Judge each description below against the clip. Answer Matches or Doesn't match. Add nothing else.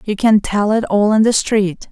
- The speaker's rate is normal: Doesn't match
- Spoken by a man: Doesn't match